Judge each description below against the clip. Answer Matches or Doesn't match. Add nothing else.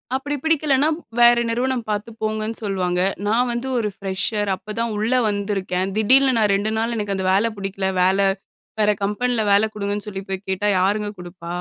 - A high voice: Matches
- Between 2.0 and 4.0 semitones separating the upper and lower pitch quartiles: Matches